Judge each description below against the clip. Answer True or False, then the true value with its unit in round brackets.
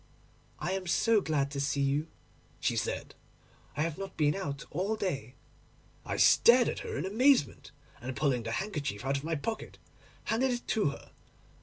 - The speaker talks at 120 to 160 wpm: False (175 wpm)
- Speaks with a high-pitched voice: False (155 Hz)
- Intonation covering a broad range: True (6.7 semitones)